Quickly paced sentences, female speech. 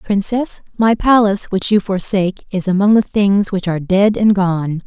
No: average, 185 wpm; female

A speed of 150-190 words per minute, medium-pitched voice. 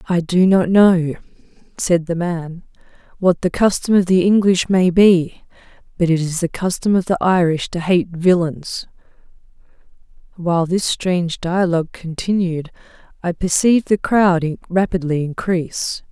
No: average, 140 wpm; medium, 175 Hz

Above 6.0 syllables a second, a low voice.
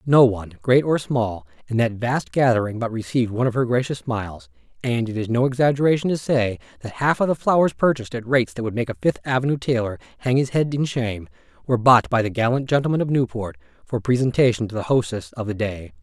Yes: 6.3 syllables/s; low, 120 Hz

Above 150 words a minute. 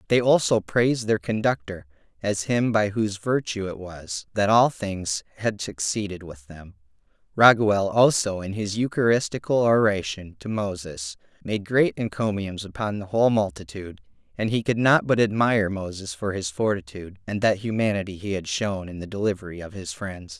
Yes: average, 165 wpm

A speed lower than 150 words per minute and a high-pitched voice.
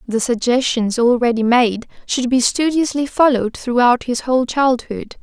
Yes: average, 140 wpm; high, 245 Hz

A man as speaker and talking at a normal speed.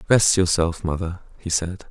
Yes: male; average, 155 wpm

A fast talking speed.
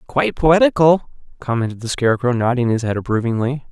No: average, 145 wpm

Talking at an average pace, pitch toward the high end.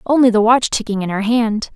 No: fast, 240 wpm; high, 225 Hz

